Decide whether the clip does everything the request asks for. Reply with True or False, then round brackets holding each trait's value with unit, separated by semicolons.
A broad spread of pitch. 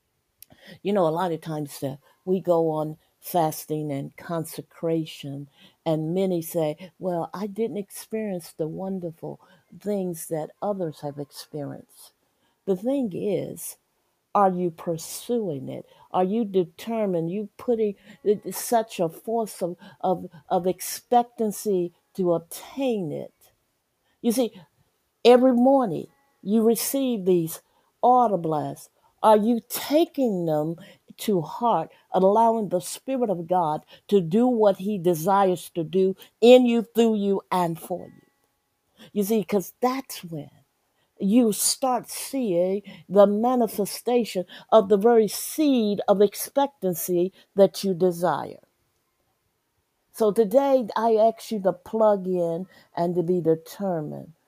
False (4.6 semitones)